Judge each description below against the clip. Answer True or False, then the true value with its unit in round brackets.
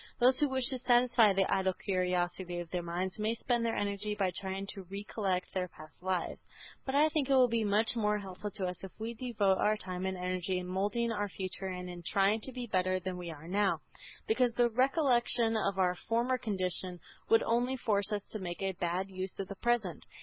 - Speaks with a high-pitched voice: True (200 Hz)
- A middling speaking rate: False (215 wpm)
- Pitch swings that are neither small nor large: True (4.0 semitones)